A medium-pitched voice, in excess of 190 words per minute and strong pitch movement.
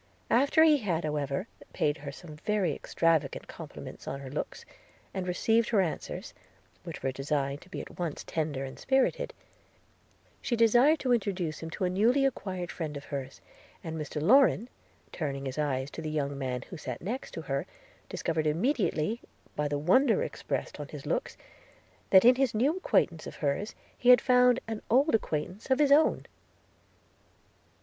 No: medium, 180 Hz; average, 170 wpm; wide, 8.3 semitones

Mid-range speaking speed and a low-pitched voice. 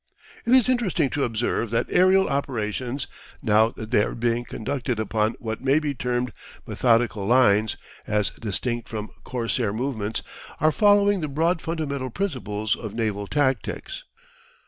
Yes: average, 145 wpm; low, 120 Hz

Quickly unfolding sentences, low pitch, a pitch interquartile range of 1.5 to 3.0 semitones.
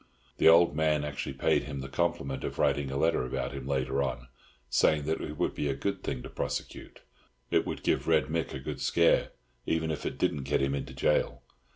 Yes: fast, 210 wpm; very low, 70 Hz; narrow, 2.5 semitones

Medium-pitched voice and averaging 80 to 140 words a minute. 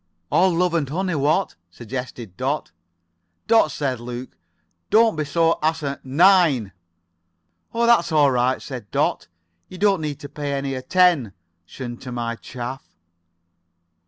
Yes: medium, 145 Hz; slow, 135 wpm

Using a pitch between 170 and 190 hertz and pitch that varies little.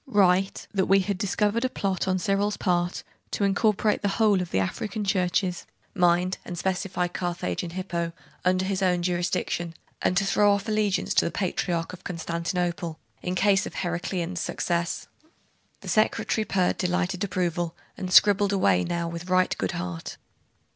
Yes: medium, 185 Hz; narrow, 2.2 semitones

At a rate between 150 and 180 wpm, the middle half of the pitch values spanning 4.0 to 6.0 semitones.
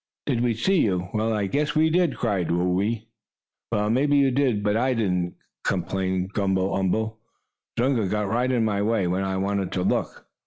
No: average, 190 wpm; average, 4.3 semitones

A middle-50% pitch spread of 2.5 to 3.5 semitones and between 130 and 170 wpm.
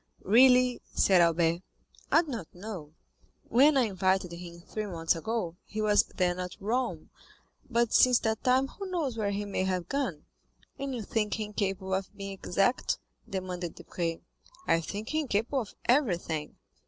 No: average, 5.2 semitones; average, 165 wpm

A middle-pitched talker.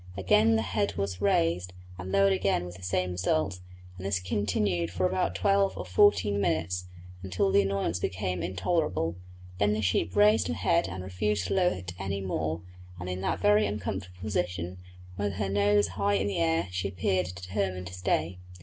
No: very low, 95 Hz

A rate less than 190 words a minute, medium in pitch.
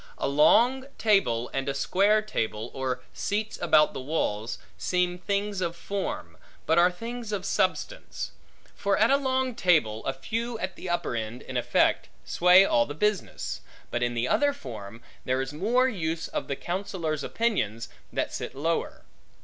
Yes: average, 165 wpm; medium, 175 Hz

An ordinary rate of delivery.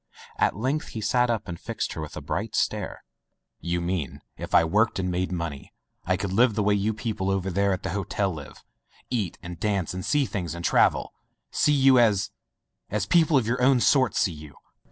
No: fast, 215 wpm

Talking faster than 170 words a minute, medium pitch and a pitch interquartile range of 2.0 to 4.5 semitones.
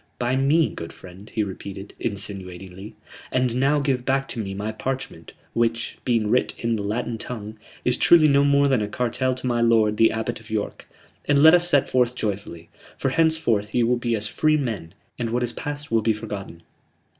No: average, 200 wpm; low, 115 Hz; average, 3.9 semitones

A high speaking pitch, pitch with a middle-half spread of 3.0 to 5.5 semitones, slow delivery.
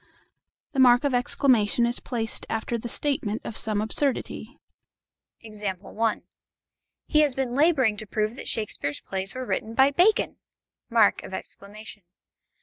Yes: high, 235 Hz; average, 3.8 semitones; slow, 120 wpm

